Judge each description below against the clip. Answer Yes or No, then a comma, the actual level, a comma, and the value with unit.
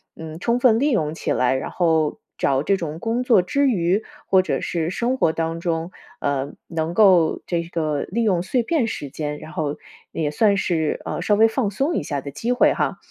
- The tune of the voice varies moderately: No, wide, 6.1 semitones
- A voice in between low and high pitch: Yes, medium, 170 Hz